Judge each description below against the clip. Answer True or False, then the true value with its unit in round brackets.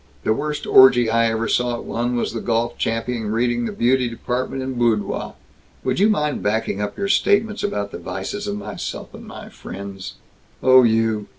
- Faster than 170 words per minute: True (190 wpm)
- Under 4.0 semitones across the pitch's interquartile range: True (2.7 semitones)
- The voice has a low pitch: True (120 Hz)